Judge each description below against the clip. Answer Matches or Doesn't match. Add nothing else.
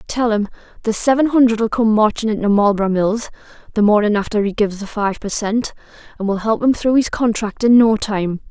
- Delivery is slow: Doesn't match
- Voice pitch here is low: Doesn't match